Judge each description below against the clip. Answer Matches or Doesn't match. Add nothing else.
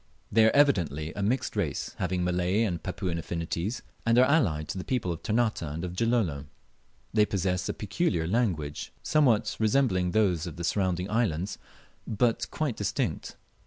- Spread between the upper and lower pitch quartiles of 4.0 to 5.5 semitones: Matches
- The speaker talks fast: Doesn't match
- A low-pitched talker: Matches